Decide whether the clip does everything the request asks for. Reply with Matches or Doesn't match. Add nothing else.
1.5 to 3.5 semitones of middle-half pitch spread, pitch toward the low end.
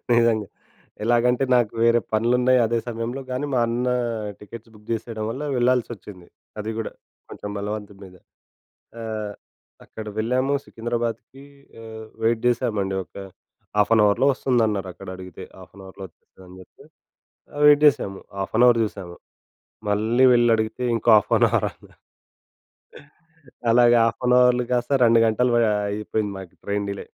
Matches